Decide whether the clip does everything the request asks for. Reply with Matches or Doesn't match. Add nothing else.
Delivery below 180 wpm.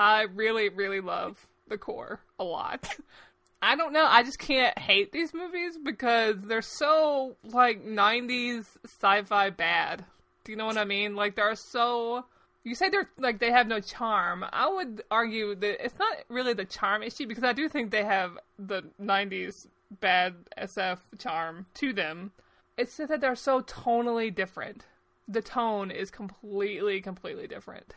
Matches